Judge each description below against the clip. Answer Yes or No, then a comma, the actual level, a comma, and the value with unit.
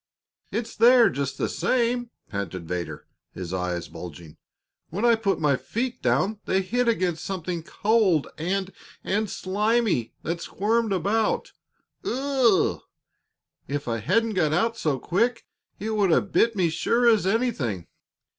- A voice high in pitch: Yes, high, 195 Hz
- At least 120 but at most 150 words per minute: Yes, average, 140 wpm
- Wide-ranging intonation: Yes, wide, 7.9 semitones